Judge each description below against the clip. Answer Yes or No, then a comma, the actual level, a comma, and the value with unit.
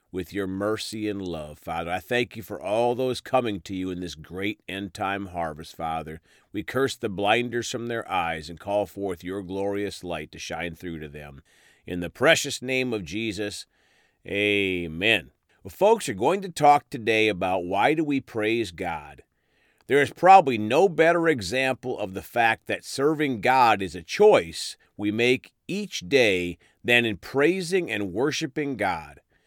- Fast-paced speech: No, average, 175 wpm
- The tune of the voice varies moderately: No, wide, 5.8 semitones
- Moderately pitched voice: No, low, 105 Hz